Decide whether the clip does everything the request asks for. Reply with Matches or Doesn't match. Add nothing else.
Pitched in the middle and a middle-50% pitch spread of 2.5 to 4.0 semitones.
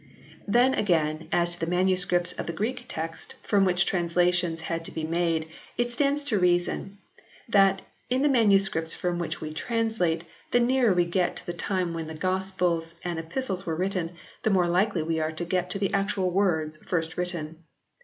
Matches